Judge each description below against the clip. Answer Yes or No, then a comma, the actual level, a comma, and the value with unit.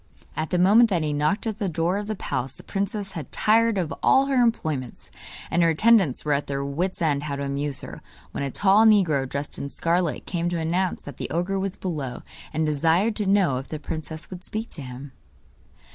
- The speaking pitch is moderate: Yes, medium, 170 Hz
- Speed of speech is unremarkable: No, fast, 220 wpm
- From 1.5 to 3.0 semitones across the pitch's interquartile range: No, average, 5.3 semitones